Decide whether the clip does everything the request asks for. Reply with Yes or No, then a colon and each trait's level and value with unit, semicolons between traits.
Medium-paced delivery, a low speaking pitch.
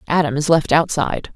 No: average, 175 wpm; medium, 155 Hz